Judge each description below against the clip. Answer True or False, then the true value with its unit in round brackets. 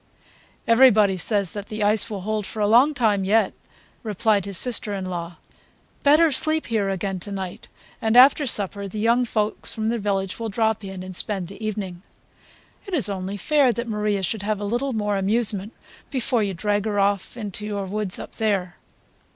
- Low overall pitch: False (210 Hz)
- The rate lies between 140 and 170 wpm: False (190 wpm)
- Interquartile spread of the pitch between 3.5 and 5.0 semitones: False (2.5 semitones)